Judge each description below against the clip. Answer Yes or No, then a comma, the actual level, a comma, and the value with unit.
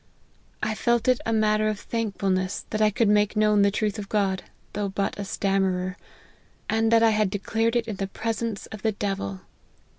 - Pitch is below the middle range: No, high, 210 Hz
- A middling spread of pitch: No, narrow, 2.2 semitones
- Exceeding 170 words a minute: Yes, average, 190 wpm